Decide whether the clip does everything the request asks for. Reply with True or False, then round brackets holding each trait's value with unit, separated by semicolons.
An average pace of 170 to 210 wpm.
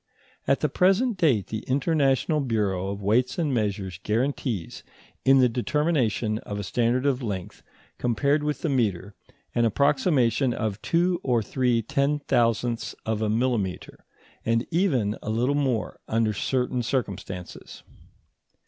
False (140 wpm)